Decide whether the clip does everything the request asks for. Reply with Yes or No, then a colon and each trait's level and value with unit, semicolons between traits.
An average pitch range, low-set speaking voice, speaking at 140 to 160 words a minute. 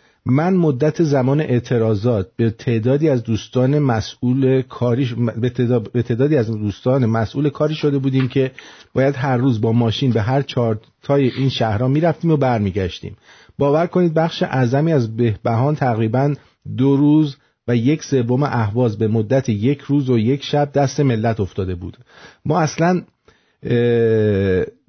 Yes: average, 3.7 semitones; low, 130 Hz; average, 150 wpm